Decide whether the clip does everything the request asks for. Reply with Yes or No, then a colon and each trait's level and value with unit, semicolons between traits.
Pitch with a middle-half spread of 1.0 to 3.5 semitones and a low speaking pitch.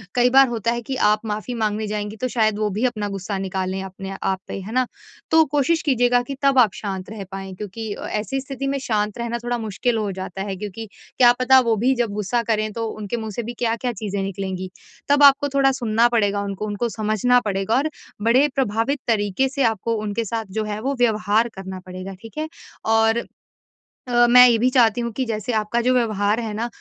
No: average, 3.1 semitones; high, 225 Hz